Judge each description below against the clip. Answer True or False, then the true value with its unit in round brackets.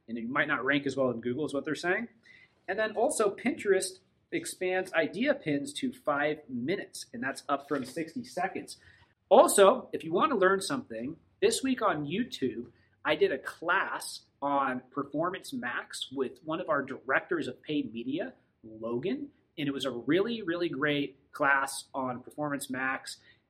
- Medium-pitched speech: True (150 Hz)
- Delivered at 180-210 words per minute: False (170 wpm)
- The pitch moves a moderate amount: False (8.0 semitones)